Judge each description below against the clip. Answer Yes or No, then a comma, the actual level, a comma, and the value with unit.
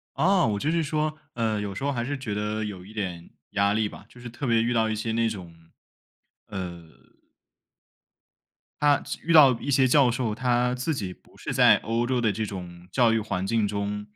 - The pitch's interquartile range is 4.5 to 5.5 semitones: No, average, 3.7 semitones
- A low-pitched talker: Yes, low, 115 Hz